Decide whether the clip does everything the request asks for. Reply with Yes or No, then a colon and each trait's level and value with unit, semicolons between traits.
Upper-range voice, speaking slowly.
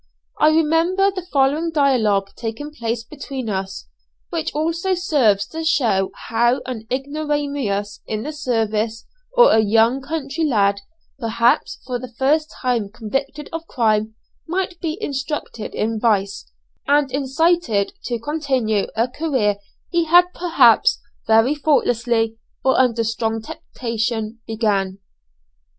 Yes: very high, 250 Hz; slow, 125 wpm